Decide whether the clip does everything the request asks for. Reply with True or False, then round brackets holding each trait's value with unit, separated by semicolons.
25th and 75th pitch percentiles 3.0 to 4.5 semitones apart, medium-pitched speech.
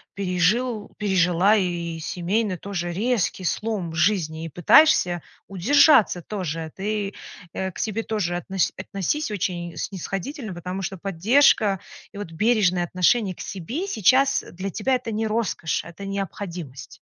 False (3.7 semitones; 195 Hz)